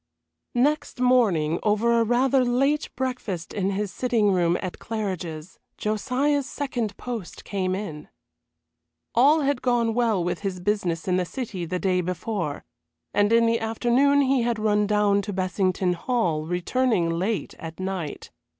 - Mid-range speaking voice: No, high, 210 Hz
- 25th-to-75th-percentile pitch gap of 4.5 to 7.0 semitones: Yes, average, 5.1 semitones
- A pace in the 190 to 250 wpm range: No, average, 150 wpm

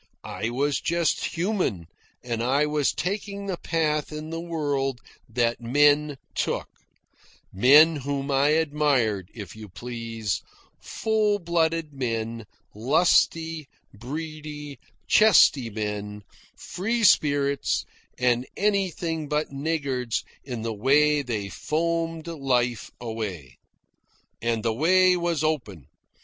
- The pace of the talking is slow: Yes, slow, 110 wpm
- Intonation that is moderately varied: No, wide, 5.7 semitones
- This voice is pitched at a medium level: Yes, medium, 145 Hz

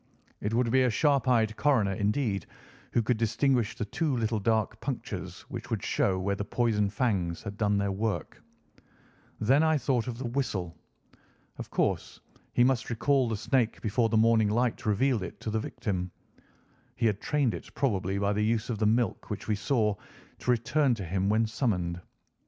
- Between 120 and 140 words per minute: No, average, 185 wpm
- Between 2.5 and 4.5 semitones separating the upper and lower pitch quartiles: Yes, average, 3.4 semitones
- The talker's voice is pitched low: Yes, low, 110 Hz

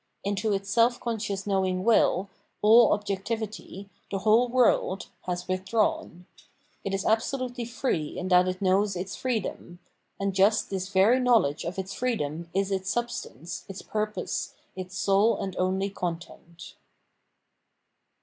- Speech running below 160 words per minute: Yes, slow, 135 wpm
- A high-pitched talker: Yes, high, 195 Hz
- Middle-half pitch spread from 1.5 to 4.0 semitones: Yes, average, 3.3 semitones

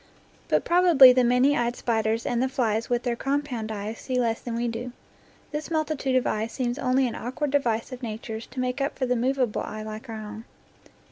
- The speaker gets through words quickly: Yes, fast, 210 wpm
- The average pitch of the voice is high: Yes, high, 245 Hz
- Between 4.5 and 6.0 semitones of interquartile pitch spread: No, average, 2.7 semitones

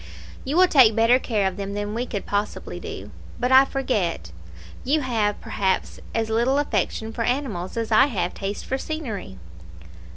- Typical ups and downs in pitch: Yes, average, 4.4 semitones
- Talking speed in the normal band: Yes, average, 170 wpm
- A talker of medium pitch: No, high, 225 Hz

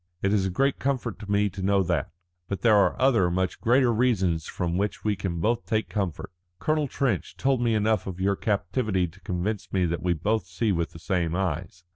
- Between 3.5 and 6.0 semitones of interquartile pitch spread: Yes, average, 3.8 semitones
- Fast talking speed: Yes, fast, 215 wpm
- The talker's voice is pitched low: Yes, low, 100 Hz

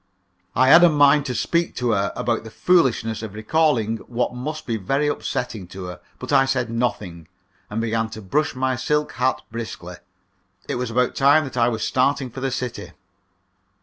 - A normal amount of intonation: Yes, average, 3.7 semitones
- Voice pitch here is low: Yes, low, 125 Hz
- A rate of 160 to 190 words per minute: Yes, average, 185 wpm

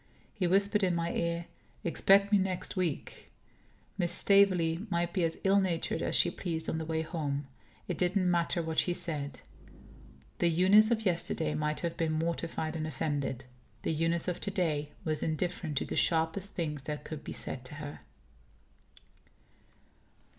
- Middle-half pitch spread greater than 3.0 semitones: No, average, 2.7 semitones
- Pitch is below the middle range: No, medium, 170 Hz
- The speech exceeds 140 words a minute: Yes, average, 165 wpm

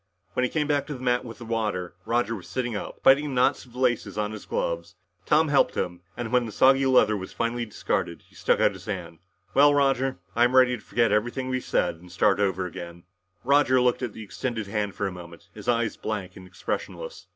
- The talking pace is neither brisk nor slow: No, fast, 230 wpm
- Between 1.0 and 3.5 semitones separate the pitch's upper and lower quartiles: No, average, 4.6 semitones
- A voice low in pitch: Yes, low, 115 Hz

